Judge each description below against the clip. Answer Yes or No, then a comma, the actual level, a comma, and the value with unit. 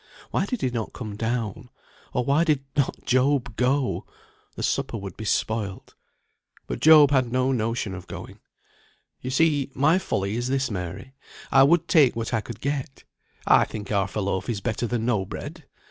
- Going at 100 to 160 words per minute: No, average, 180 wpm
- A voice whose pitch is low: Yes, low, 125 Hz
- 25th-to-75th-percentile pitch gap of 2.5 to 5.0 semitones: Yes, average, 4.2 semitones